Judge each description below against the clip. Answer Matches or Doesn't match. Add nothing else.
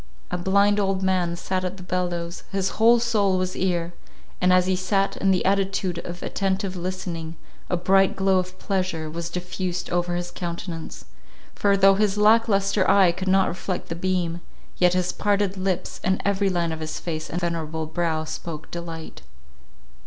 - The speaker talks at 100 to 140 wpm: Doesn't match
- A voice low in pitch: Doesn't match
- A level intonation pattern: Matches